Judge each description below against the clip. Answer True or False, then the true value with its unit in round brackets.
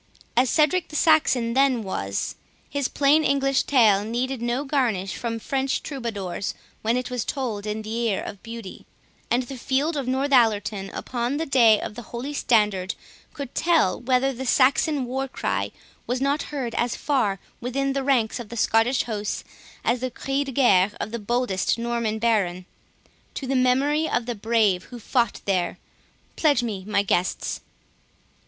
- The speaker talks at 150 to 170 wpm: True (165 wpm)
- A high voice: True (240 Hz)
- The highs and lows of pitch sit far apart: False (3.9 semitones)